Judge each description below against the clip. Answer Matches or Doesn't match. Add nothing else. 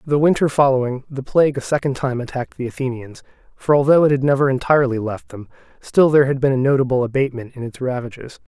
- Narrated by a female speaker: Doesn't match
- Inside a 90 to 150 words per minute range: Doesn't match